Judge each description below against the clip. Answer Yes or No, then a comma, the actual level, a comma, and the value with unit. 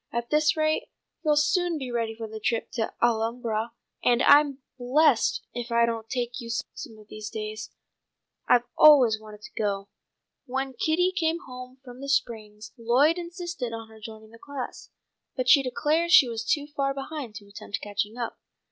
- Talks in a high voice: Yes, high, 245 Hz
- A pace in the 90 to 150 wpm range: No, average, 180 wpm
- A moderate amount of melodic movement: Yes, average, 4.6 semitones